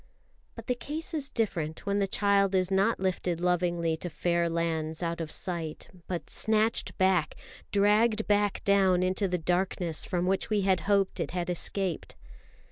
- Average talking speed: Yes, average, 165 wpm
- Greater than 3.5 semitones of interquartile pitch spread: No, average, 2.8 semitones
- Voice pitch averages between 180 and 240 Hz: Yes, medium, 185 Hz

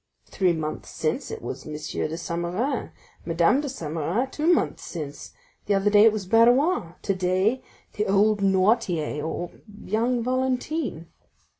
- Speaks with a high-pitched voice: Yes, high, 195 Hz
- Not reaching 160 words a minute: Yes, average, 150 wpm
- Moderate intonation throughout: No, wide, 6.4 semitones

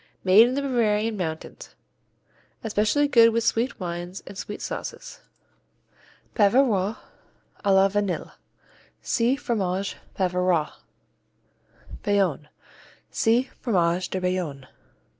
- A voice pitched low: No, high, 200 Hz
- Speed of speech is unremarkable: No, slow, 100 wpm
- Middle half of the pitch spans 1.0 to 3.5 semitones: No, average, 4.0 semitones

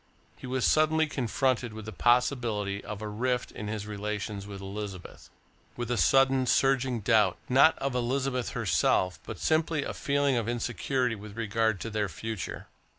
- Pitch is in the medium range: No, low, 115 Hz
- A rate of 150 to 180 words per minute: Yes, average, 160 wpm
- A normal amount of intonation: Yes, average, 3.8 semitones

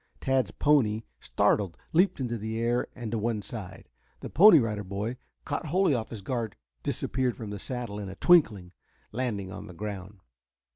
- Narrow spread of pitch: No, average, 3.8 semitones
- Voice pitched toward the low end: Yes, low, 115 Hz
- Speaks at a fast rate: No, average, 175 wpm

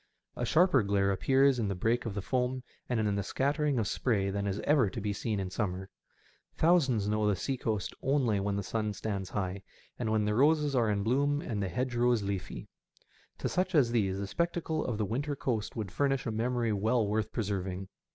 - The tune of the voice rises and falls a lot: No, average, 4.6 semitones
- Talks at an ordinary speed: No, fast, 210 wpm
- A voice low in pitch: Yes, low, 110 Hz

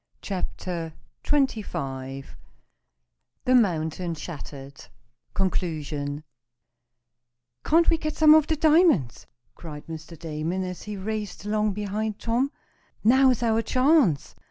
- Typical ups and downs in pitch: No, wide, 8.1 semitones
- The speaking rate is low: Yes, slow, 105 wpm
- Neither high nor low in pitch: No, high, 195 Hz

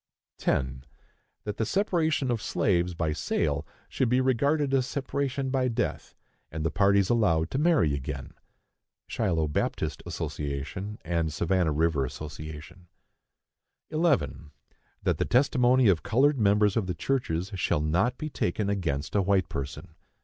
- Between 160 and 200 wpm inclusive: No, average, 140 wpm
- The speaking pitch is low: Yes, low, 100 Hz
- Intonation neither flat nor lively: No, wide, 8.3 semitones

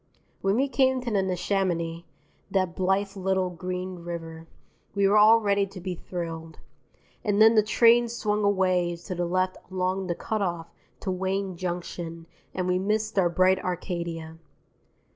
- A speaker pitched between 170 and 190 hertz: Yes, medium, 185 Hz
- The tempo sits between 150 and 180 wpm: Yes, average, 160 wpm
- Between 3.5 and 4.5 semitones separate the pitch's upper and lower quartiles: No, narrow, 2.5 semitones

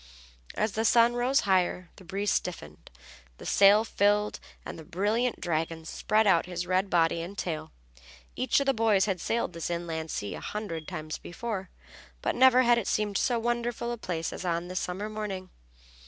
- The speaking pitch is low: No, high, 195 Hz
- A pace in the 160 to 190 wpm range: Yes, average, 185 wpm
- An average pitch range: Yes, average, 4.6 semitones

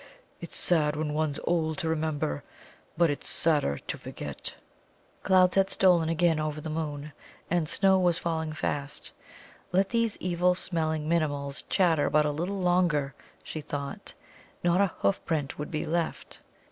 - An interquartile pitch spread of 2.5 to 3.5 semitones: Yes, average, 2.8 semitones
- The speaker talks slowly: No, average, 155 wpm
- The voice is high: No, medium, 160 Hz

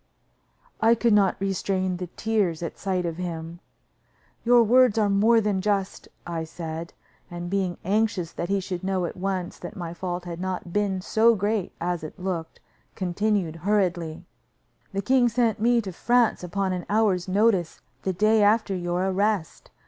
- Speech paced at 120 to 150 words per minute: No, average, 165 wpm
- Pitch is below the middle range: No, high, 190 Hz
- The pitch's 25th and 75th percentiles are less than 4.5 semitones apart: Yes, average, 3.3 semitones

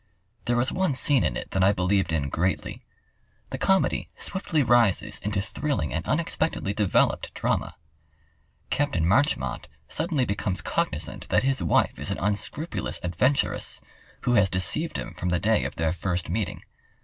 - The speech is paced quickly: No, average, 155 wpm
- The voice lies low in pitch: Yes, low, 100 Hz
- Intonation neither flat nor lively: No, wide, 6.8 semitones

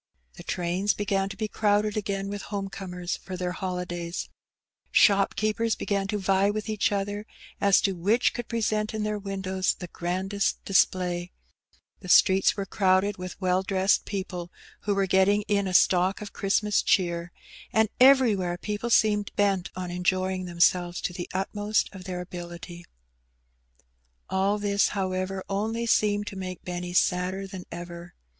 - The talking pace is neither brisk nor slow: Yes, average, 155 wpm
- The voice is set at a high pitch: Yes, high, 195 Hz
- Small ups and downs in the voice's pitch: Yes, narrow, 2.2 semitones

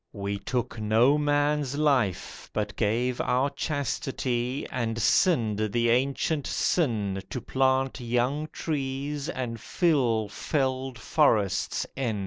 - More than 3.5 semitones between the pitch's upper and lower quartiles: Yes, average, 3.9 semitones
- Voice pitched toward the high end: No, low, 125 Hz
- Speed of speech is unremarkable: No, slow, 115 wpm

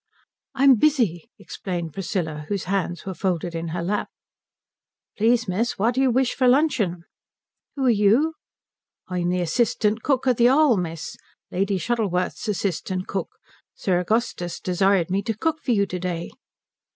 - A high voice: Yes, high, 195 Hz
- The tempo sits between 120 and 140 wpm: No, average, 155 wpm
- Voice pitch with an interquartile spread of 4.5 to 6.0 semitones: Yes, average, 5.3 semitones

